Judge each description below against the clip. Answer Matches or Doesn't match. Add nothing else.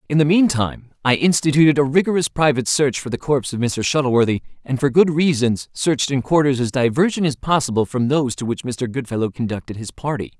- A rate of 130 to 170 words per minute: Doesn't match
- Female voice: Doesn't match